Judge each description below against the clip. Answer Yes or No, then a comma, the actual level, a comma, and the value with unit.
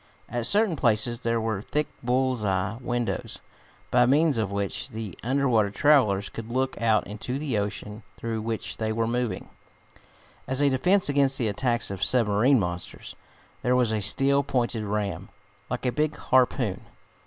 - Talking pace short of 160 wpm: No, average, 165 wpm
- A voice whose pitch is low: Yes, low, 120 Hz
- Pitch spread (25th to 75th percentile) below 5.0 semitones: Yes, average, 3.6 semitones